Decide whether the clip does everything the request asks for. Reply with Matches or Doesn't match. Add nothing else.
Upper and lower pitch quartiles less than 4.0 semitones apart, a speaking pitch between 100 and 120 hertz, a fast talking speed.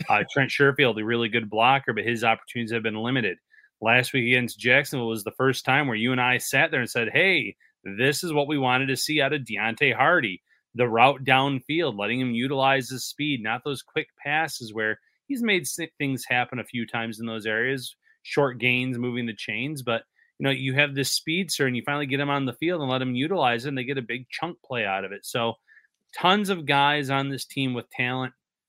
Doesn't match